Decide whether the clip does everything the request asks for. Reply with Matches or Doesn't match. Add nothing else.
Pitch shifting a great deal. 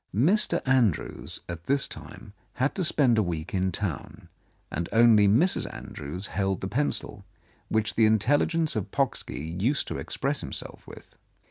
Matches